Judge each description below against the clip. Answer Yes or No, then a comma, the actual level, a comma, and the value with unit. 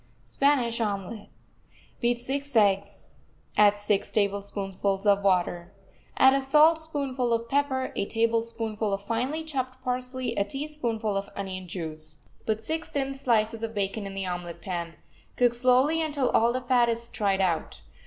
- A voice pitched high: Yes, high, 230 Hz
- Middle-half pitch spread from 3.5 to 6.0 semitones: Yes, average, 4.6 semitones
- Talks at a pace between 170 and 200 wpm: No, average, 150 wpm